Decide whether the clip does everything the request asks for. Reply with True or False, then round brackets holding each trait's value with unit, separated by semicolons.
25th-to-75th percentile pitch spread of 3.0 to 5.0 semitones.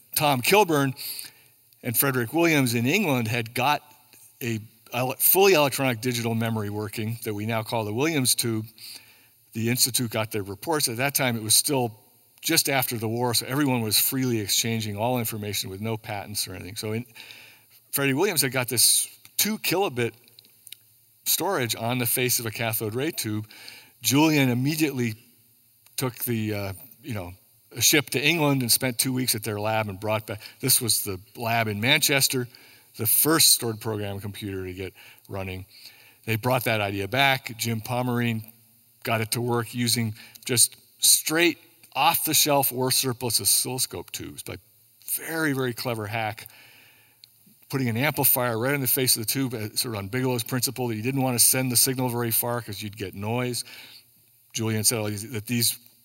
False (2.6 semitones)